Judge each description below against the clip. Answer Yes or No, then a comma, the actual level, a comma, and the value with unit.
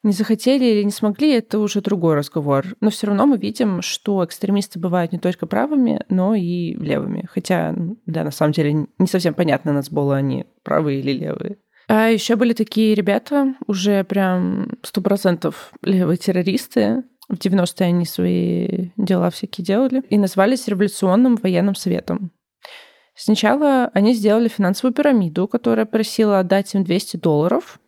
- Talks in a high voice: Yes, high, 200 Hz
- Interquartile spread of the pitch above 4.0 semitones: No, average, 3.7 semitones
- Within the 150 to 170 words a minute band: Yes, average, 155 wpm